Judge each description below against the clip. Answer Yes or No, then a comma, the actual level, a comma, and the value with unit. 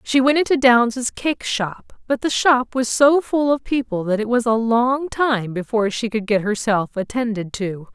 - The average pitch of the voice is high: Yes, high, 235 Hz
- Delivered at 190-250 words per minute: Yes, fast, 205 wpm